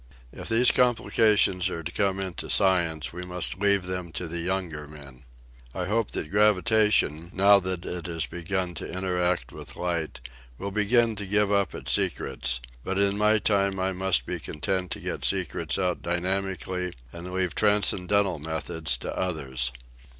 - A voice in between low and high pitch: No, very low, 90 Hz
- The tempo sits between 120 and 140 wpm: No, average, 170 wpm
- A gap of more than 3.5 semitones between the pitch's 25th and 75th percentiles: No, average, 2.8 semitones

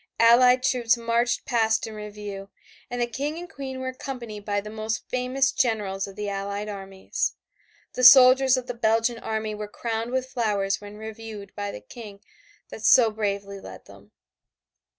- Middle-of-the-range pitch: No, high, 225 Hz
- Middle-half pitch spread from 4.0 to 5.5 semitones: No, average, 3.3 semitones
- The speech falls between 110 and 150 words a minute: No, average, 170 wpm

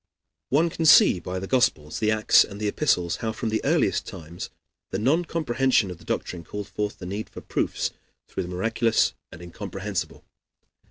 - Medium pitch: No, low, 105 Hz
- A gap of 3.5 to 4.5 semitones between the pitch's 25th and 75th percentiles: No, average, 5.0 semitones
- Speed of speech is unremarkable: Yes, average, 180 wpm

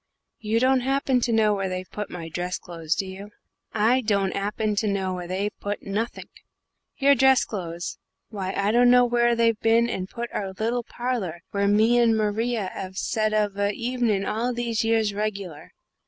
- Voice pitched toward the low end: No, high, 215 Hz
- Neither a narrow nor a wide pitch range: Yes, average, 3.3 semitones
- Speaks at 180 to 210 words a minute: Yes, average, 185 wpm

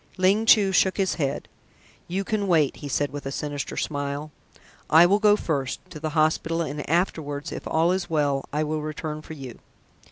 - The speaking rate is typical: Yes, average, 190 wpm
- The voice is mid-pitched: Yes, medium, 155 Hz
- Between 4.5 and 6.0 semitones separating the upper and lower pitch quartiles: No, average, 4.0 semitones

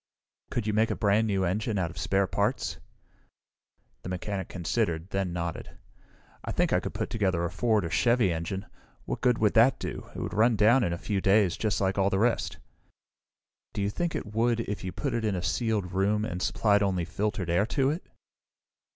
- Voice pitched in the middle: No, low, 100 Hz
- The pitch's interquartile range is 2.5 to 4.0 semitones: Yes, average, 3.3 semitones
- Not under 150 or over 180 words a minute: No, fast, 205 wpm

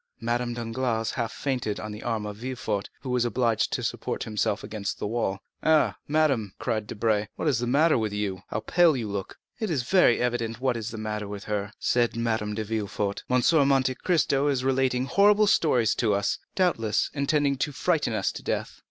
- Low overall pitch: Yes, low, 120 Hz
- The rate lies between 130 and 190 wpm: No, average, 200 wpm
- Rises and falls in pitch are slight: No, average, 4.1 semitones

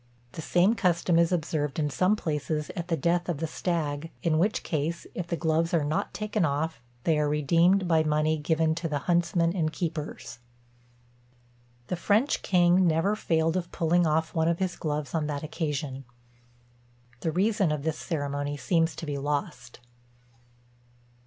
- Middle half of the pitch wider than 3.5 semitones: No, narrow, 2.5 semitones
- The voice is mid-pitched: Yes, medium, 160 Hz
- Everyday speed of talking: Yes, average, 165 wpm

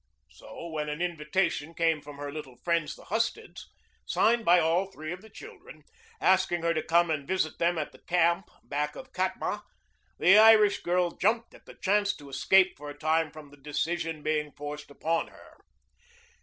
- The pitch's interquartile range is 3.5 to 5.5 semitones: Yes, average, 4.0 semitones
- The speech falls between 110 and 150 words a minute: No, average, 185 wpm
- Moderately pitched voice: Yes, medium, 170 Hz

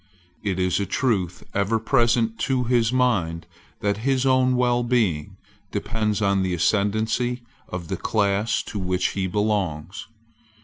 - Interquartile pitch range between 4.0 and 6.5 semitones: Yes, average, 4.4 semitones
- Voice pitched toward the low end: Yes, low, 105 Hz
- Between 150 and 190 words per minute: No, slow, 135 wpm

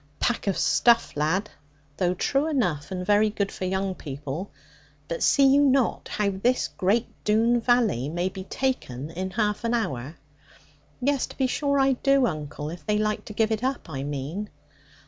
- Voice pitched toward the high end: Yes, high, 205 Hz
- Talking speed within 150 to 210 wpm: Yes, average, 180 wpm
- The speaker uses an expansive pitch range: Yes, wide, 6.0 semitones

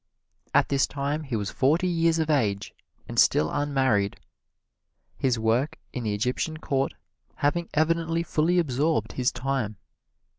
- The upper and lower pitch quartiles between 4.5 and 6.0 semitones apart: Yes, average, 5.1 semitones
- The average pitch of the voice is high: No, medium, 140 Hz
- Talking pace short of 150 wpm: Yes, average, 140 wpm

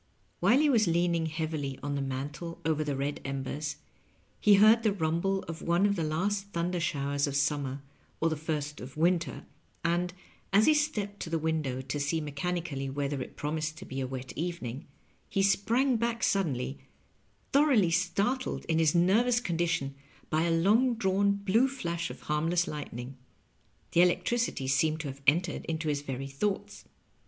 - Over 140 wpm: Yes, average, 175 wpm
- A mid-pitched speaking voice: Yes, medium, 165 Hz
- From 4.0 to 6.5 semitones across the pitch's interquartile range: Yes, average, 5.3 semitones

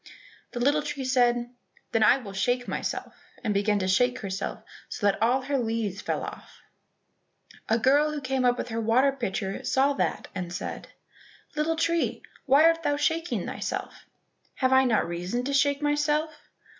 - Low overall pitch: No, very high, 255 Hz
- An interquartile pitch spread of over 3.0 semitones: Yes, average, 4.5 semitones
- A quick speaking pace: No, average, 170 wpm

